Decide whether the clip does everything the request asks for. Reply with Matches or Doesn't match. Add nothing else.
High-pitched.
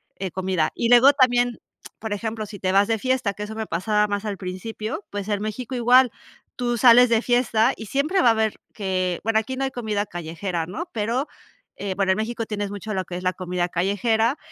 Matches